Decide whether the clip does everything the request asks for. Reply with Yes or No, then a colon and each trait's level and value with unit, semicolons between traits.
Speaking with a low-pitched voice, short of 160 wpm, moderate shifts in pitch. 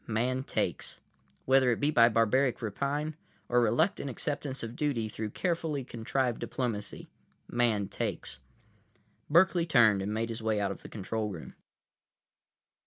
Yes: low, 120 Hz; average, 140 wpm; average, 4.0 semitones